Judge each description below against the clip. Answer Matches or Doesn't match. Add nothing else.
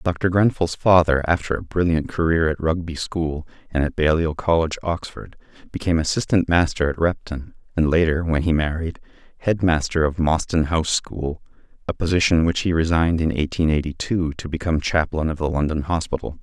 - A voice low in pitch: Matches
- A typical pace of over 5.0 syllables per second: Matches